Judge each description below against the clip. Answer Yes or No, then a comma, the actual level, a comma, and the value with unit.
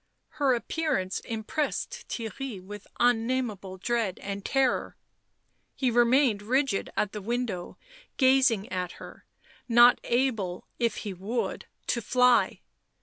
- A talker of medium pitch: No, high, 235 Hz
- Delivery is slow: Yes, slow, 115 wpm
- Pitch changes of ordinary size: Yes, average, 4.2 semitones